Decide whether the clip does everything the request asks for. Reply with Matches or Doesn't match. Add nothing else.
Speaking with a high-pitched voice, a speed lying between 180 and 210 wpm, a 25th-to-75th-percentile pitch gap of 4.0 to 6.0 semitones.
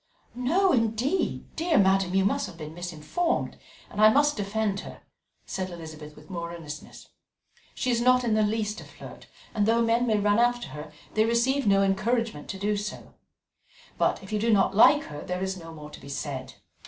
Matches